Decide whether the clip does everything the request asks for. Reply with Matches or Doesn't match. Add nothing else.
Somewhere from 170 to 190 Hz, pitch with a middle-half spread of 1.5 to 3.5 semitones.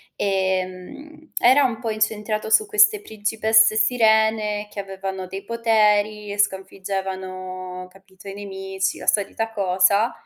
Doesn't match